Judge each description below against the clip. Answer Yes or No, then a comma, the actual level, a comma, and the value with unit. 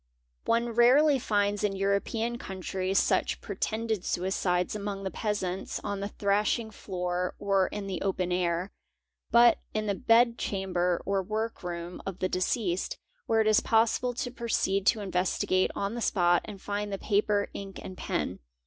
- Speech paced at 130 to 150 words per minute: No, average, 160 wpm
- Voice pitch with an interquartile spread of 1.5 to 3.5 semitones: Yes, average, 2.9 semitones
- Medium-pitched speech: No, high, 200 Hz